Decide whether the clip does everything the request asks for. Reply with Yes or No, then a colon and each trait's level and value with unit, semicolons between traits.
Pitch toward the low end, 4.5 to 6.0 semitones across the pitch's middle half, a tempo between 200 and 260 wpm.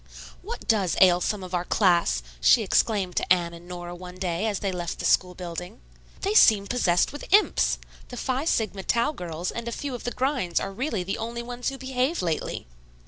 No: high, 195 Hz; wide, 5.4 semitones; fast, 205 wpm